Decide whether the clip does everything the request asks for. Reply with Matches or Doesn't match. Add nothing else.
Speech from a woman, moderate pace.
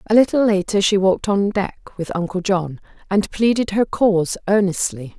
Matches